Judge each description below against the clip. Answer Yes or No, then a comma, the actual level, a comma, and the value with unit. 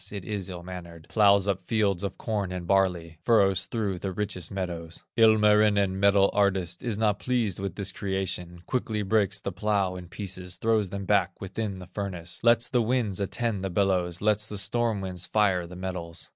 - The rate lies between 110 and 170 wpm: No, average, 185 wpm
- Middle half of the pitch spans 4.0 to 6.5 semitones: No, narrow, 2.5 semitones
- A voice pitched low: Yes, low, 100 Hz